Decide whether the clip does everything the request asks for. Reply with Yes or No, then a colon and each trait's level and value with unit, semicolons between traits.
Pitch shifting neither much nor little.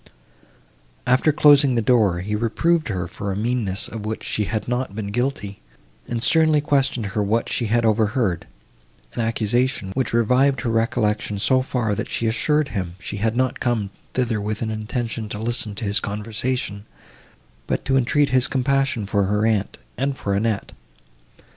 Yes: average, 3.6 semitones